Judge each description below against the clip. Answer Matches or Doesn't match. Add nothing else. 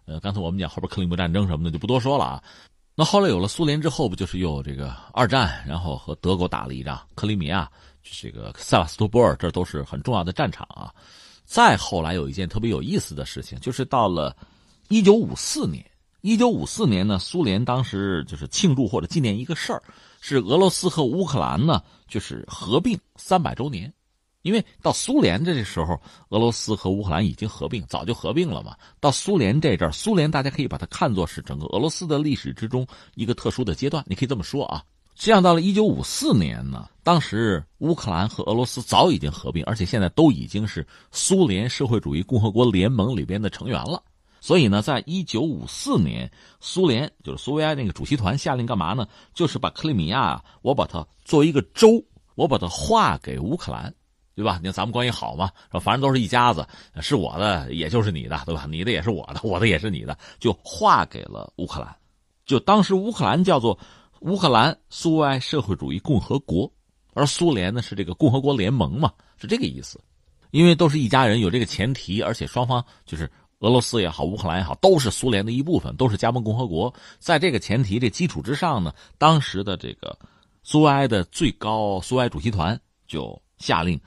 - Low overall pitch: Matches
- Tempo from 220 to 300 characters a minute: Doesn't match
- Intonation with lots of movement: Matches